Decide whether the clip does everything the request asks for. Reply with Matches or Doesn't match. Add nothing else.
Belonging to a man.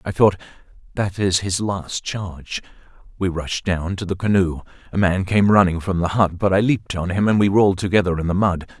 Matches